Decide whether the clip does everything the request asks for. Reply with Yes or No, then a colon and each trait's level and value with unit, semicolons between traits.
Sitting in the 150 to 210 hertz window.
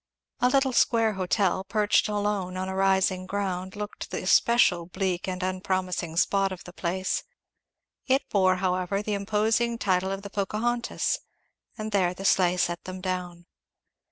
Yes: high, 190 Hz